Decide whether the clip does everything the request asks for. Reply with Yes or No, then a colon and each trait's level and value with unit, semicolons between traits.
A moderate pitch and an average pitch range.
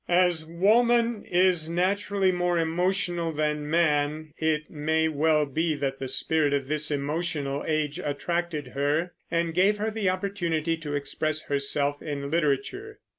Yes: medium, 160 Hz; average, 3.2 semitones